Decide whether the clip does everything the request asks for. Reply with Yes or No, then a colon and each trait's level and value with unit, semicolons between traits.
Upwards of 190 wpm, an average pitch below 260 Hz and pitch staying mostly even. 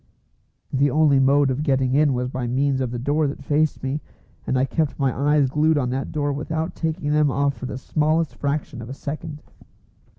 Yes: fast, 205 wpm; medium, 140 Hz; narrow, 2.3 semitones